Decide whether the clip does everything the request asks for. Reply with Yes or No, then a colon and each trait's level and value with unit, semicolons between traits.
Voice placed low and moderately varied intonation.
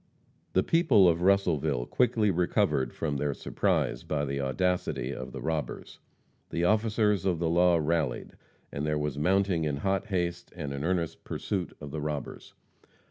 Yes: very low, 85 Hz; average, 4.3 semitones